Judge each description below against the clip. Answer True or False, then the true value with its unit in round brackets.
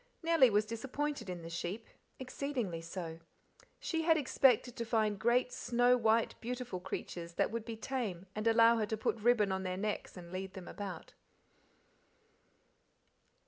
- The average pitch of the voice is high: True (220 Hz)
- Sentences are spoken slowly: False (155 wpm)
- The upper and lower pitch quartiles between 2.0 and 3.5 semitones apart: False (4.5 semitones)